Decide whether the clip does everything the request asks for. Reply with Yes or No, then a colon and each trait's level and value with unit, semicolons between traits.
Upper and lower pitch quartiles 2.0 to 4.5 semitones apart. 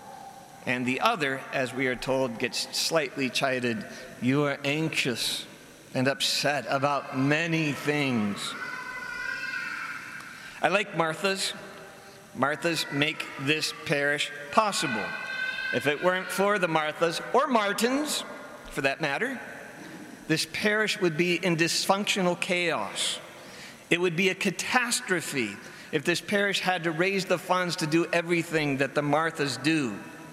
No: wide, 5.5 semitones